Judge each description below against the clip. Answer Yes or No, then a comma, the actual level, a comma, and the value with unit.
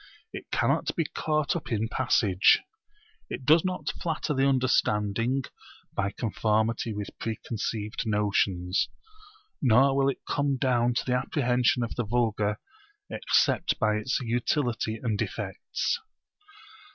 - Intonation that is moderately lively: Yes, average, 4.0 semitones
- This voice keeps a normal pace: No, slow, 125 wpm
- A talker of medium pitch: No, low, 120 Hz